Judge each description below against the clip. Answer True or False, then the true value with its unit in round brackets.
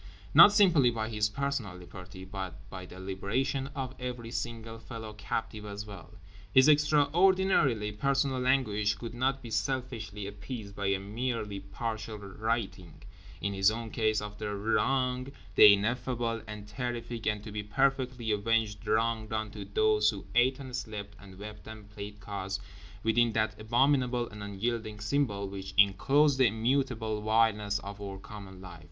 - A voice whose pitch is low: True (110 Hz)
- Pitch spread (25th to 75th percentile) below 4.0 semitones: True (3.4 semitones)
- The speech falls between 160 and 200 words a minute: False (150 wpm)